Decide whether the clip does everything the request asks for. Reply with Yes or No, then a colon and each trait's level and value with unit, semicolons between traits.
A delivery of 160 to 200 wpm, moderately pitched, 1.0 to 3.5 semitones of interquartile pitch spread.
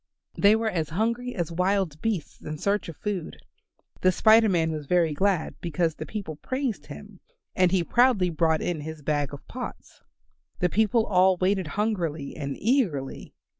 No: average, 170 wpm; medium, 180 Hz; average, 5.0 semitones